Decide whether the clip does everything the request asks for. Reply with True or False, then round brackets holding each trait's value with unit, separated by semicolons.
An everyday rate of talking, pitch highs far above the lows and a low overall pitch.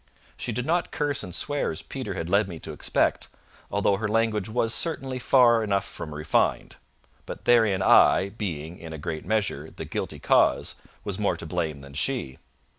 True (185 wpm; 6.0 semitones; 100 Hz)